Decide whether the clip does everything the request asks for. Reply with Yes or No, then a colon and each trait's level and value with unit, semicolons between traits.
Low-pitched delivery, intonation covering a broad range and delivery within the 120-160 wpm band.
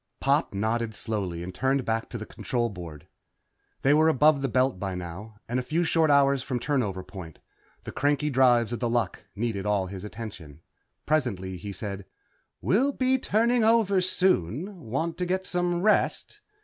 No: low, 120 Hz; wide, 7.9 semitones; average, 175 wpm